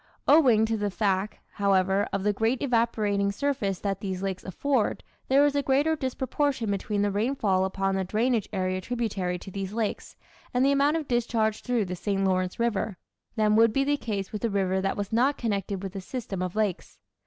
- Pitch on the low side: No, high, 210 Hz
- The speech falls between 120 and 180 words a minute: No, average, 200 wpm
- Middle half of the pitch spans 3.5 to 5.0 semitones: Yes, average, 4.0 semitones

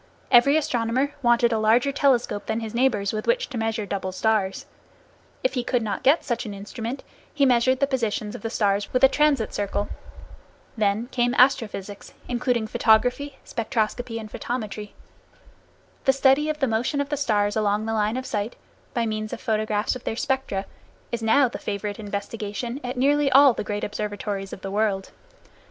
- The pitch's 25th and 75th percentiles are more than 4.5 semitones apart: No, average, 3.7 semitones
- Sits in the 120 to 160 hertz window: No, high, 230 Hz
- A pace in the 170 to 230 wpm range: Yes, average, 175 wpm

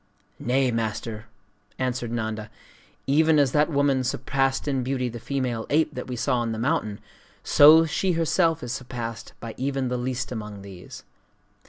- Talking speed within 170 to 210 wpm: No, average, 160 wpm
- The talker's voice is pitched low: Yes, low, 125 Hz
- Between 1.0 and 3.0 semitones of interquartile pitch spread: No, average, 3.4 semitones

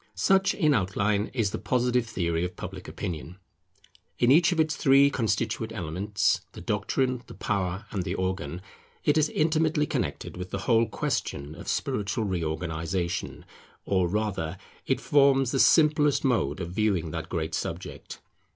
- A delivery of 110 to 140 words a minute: No, average, 150 wpm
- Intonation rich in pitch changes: Yes, wide, 7.2 semitones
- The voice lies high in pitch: No, low, 105 Hz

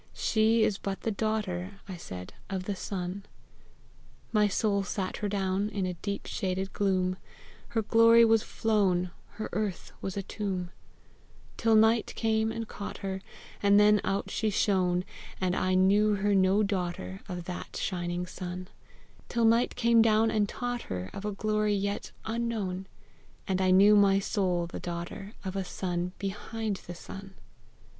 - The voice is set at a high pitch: Yes, high, 200 Hz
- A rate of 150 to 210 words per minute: Yes, average, 160 wpm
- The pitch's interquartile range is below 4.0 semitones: Yes, narrow, 2.6 semitones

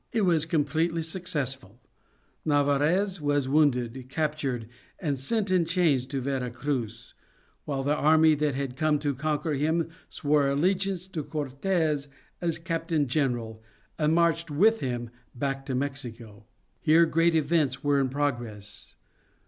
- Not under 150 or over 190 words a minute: No, slow, 135 wpm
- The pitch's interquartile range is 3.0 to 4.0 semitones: Yes, average, 3.5 semitones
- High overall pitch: No, medium, 145 Hz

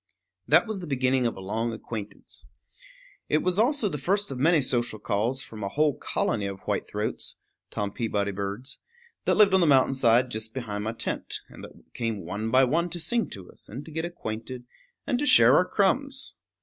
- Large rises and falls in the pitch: Yes, wide, 7.7 semitones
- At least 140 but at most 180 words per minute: No, average, 200 wpm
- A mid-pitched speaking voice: No, low, 130 Hz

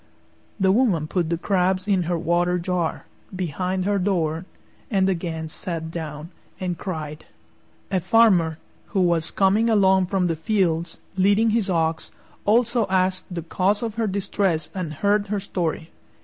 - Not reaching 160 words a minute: Yes, average, 150 wpm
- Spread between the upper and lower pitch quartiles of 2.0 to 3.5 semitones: Yes, average, 3.2 semitones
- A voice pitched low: No, medium, 185 Hz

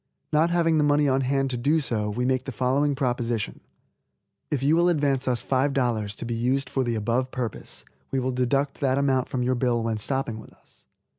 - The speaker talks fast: Yes, fast, 210 wpm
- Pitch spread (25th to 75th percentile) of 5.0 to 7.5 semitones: No, average, 2.7 semitones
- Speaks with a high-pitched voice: No, low, 130 Hz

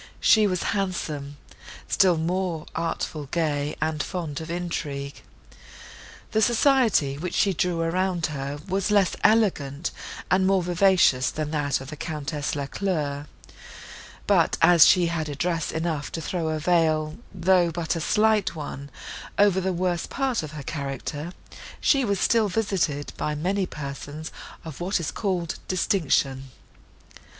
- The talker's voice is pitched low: No, medium, 165 Hz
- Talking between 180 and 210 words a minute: No, average, 140 wpm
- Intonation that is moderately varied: Yes, average, 3.9 semitones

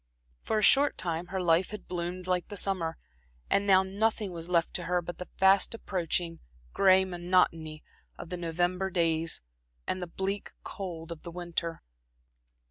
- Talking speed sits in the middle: Yes, average, 165 wpm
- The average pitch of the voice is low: No, medium, 180 Hz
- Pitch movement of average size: No, narrow, 2.2 semitones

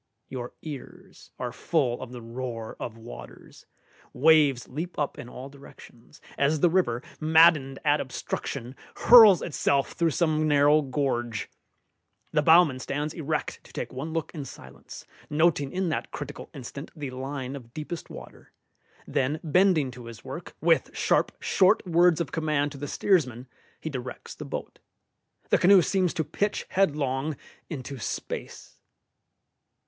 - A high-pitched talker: No, medium, 145 Hz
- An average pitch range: Yes, average, 3.8 semitones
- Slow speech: No, average, 145 wpm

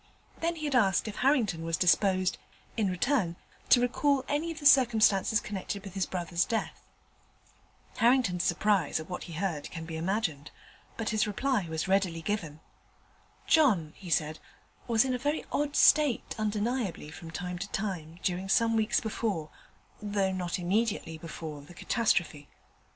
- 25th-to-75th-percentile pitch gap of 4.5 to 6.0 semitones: Yes, average, 5.3 semitones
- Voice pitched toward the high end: Yes, high, 195 Hz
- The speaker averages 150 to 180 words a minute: Yes, average, 155 wpm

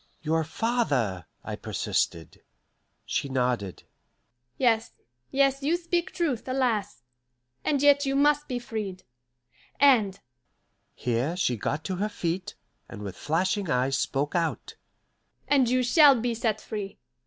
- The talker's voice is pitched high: Yes, high, 210 Hz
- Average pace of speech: No, slow, 130 wpm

